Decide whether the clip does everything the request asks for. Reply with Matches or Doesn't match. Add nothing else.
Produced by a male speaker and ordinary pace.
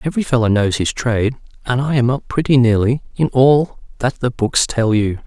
Matches